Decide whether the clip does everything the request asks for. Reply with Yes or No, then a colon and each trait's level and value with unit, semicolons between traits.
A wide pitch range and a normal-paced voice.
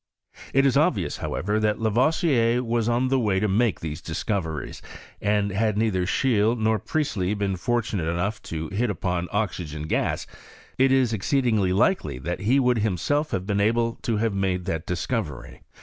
No: average, 4.4 semitones; average, 170 wpm